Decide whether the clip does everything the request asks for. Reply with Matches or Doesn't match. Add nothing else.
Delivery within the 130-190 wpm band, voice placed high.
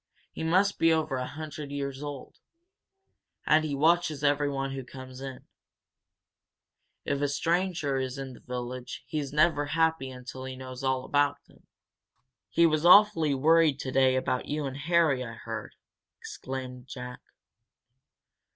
Doesn't match